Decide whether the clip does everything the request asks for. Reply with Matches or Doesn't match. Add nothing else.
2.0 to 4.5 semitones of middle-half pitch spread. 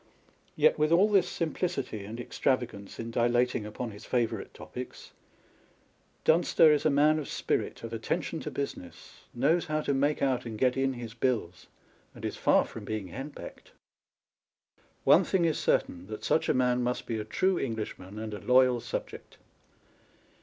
Doesn't match